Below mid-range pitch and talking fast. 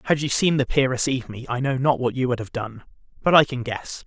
Yes: low, 130 Hz; fast, 280 wpm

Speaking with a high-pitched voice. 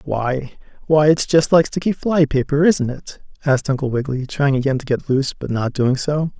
No: medium, 140 Hz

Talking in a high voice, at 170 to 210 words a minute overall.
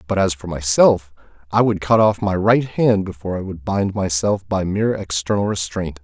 No: very low, 95 Hz; average, 200 wpm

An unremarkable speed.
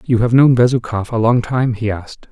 No: fast, 235 wpm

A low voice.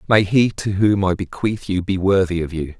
Yes: very low, 95 Hz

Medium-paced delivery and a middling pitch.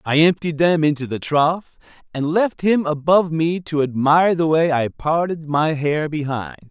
Yes: average, 180 wpm; medium, 155 Hz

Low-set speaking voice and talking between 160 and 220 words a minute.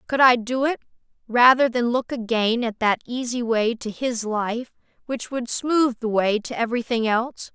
No: high, 240 Hz; average, 185 wpm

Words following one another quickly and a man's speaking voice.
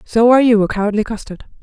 No: fast, 220 wpm; female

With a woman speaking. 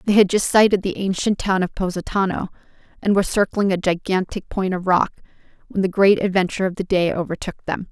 Yes: female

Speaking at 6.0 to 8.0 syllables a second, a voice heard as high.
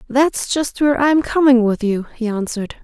No: 5.0 syllables/s; very high, 250 Hz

